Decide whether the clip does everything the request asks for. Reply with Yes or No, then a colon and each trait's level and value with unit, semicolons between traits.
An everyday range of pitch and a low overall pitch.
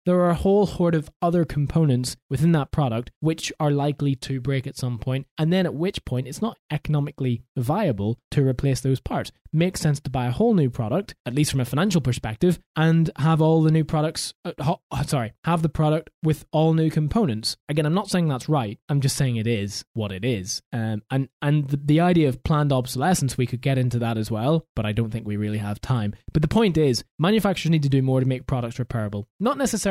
No: average, 4.3 semitones; medium, 145 Hz